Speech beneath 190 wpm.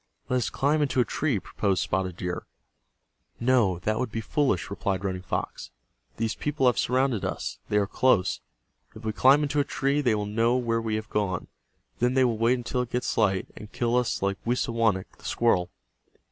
No: average, 195 wpm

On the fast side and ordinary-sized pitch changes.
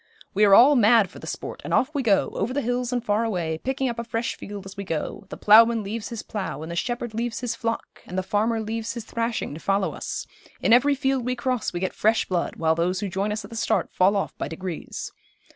Yes: fast, 255 wpm; average, 3.7 semitones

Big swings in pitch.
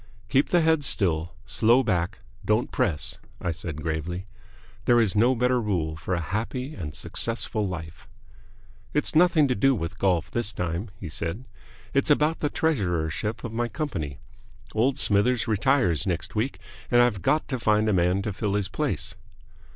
Yes: wide, 6.4 semitones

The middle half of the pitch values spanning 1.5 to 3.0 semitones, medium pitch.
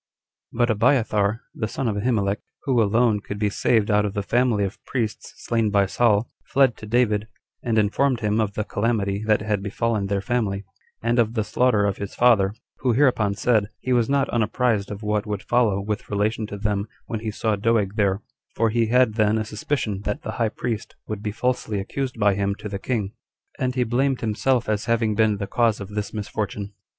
No: narrow, 2.5 semitones; low, 110 Hz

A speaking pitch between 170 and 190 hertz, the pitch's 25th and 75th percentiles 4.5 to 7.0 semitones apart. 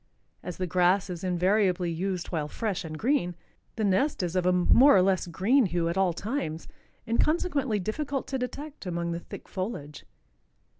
Yes: medium, 185 Hz; average, 5.0 semitones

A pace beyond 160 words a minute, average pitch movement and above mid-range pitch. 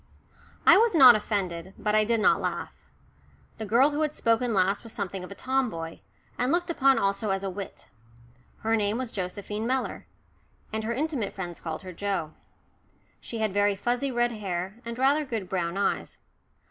Yes: average, 180 wpm; average, 4.3 semitones; high, 215 Hz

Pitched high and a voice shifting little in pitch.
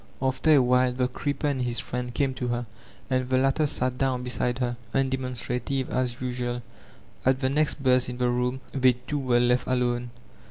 No: low, 125 Hz; narrow, 1.2 semitones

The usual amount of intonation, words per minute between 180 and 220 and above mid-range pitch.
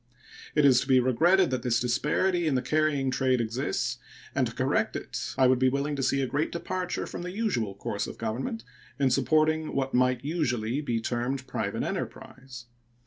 No: average, 3.6 semitones; average, 190 wpm; low, 130 Hz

